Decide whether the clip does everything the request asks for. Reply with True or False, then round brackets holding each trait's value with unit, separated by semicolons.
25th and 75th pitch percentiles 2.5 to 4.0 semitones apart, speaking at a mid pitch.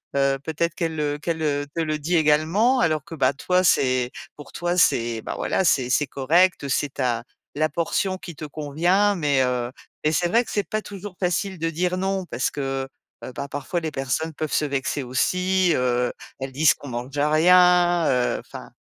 False (4.6 semitones; 155 Hz)